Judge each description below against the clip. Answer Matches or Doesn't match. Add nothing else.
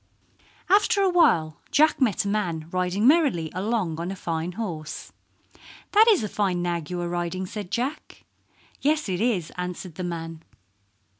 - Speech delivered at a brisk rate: Doesn't match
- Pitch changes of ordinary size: Doesn't match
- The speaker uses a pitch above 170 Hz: Matches